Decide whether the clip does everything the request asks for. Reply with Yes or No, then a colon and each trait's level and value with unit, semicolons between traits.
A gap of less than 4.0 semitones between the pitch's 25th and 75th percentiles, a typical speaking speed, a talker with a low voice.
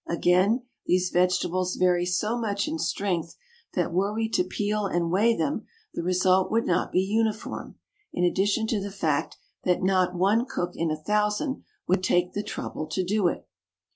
No: average, 2.9 semitones; average, 175 wpm; medium, 185 Hz